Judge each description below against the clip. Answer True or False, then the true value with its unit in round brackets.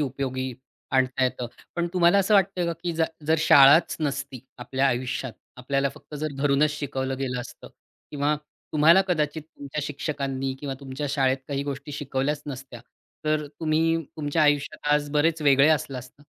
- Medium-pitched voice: True (145 Hz)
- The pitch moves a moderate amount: False (2.3 semitones)